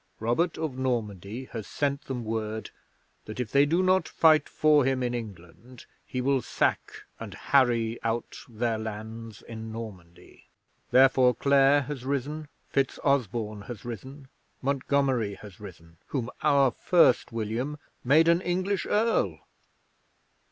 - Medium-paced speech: No, slow, 130 wpm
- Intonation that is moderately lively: Yes, average, 4.2 semitones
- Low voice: Yes, low, 125 Hz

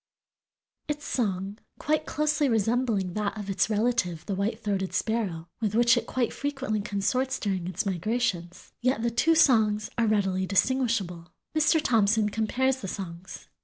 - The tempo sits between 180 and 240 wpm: No, average, 150 wpm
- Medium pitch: No, high, 215 Hz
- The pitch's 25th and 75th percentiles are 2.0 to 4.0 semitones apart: No, average, 4.4 semitones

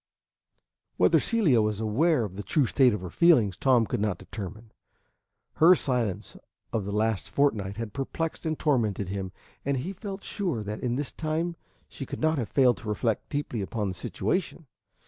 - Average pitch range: No, wide, 6.7 semitones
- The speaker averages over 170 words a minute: Yes, average, 180 wpm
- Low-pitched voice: Yes, low, 120 Hz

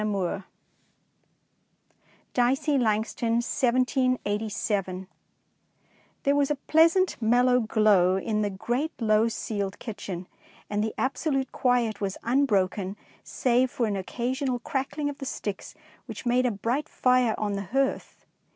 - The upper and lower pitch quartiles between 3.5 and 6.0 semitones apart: Yes, average, 4.1 semitones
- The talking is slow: Yes, slow, 130 wpm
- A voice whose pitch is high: Yes, high, 235 Hz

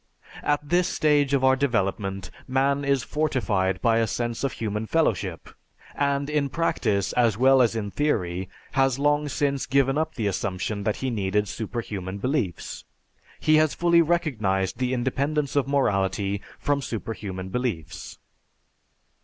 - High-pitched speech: No, low, 125 Hz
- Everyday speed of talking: Yes, average, 145 wpm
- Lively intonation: Yes, wide, 5.9 semitones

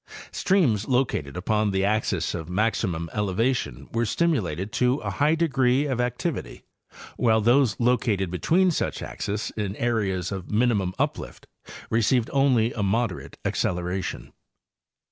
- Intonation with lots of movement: No, average, 4.6 semitones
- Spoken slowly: Yes, slow, 130 wpm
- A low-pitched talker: Yes, low, 110 Hz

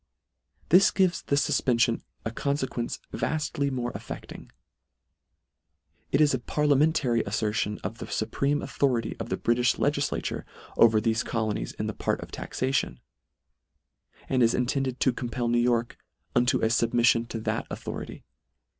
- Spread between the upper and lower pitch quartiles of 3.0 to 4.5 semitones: Yes, average, 3.3 semitones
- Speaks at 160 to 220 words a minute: No, average, 150 wpm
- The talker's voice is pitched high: No, low, 120 Hz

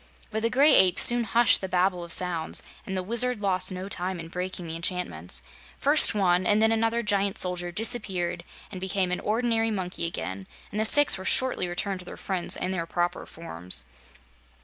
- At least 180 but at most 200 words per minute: Yes, average, 195 wpm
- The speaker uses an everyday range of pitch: Yes, average, 3.7 semitones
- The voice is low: No, medium, 185 Hz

